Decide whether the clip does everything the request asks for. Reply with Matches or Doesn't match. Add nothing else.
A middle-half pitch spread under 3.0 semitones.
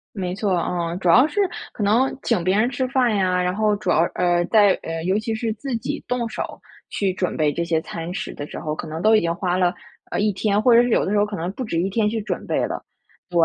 Doesn't match